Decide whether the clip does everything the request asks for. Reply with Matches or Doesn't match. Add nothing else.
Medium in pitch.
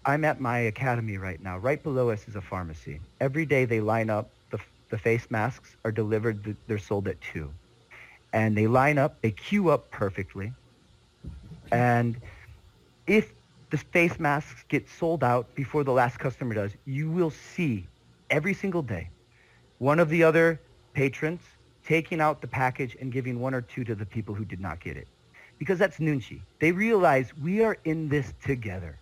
Doesn't match